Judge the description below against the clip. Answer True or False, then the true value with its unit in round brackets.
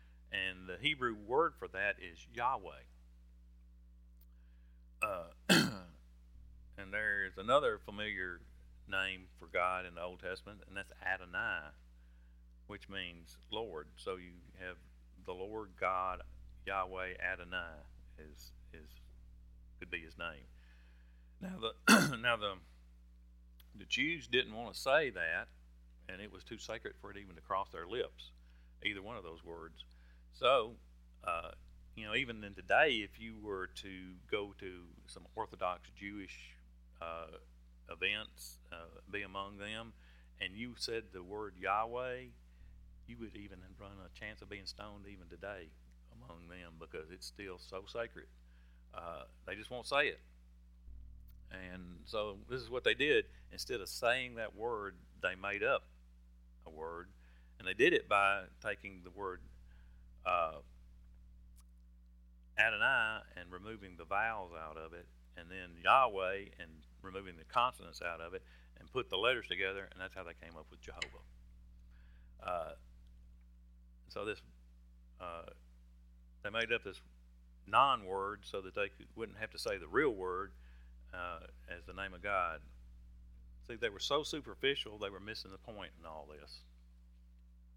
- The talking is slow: False (150 wpm)